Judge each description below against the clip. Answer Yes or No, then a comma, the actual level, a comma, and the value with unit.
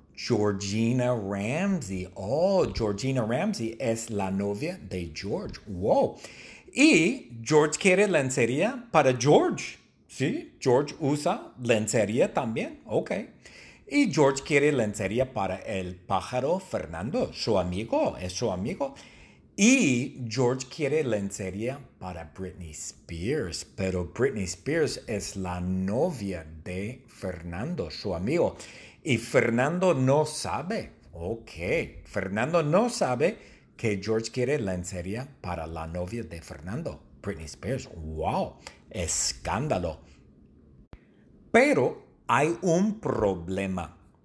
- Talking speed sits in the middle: No, slow, 105 wpm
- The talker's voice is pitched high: No, low, 105 Hz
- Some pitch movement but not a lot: No, wide, 6.3 semitones